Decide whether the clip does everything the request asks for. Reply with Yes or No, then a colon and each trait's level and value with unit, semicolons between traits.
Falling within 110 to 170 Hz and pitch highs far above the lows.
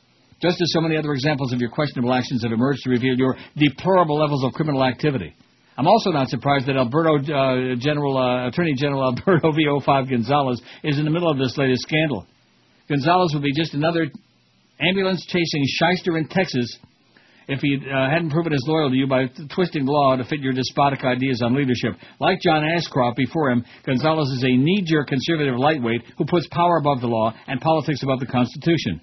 No: medium, 140 Hz; average, 3.7 semitones